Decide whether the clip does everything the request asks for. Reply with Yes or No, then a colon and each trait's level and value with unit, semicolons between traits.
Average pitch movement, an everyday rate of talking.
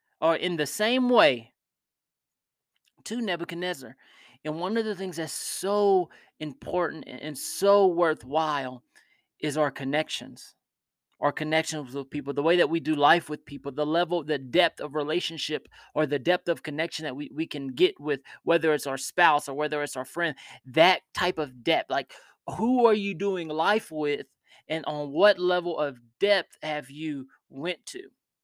Yes: average, 3.3 semitones; average, 170 wpm